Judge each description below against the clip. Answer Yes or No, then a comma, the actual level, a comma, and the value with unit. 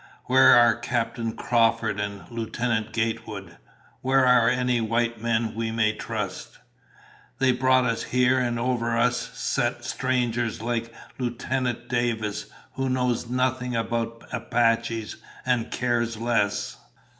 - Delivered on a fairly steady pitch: Yes, narrow, 1.7 semitones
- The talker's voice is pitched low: Yes, low, 115 Hz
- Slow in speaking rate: Yes, slow, 120 wpm